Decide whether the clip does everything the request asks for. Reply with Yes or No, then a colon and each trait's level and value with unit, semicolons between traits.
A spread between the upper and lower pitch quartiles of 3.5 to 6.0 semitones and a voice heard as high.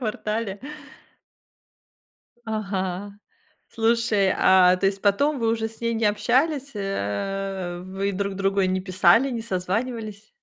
No: average, 2.9 semitones; high, 200 Hz